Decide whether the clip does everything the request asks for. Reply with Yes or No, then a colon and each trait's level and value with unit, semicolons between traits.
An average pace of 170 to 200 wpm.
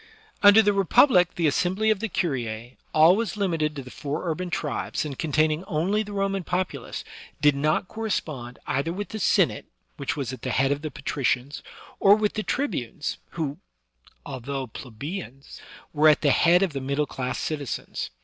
Yes: average, 175 wpm